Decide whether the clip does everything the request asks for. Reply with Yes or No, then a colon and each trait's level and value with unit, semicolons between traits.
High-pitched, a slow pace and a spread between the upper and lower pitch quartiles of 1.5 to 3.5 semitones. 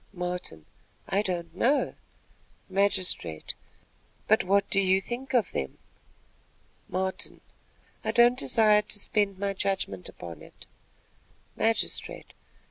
Yes: high, 195 Hz; slow, 110 wpm; average, 2.9 semitones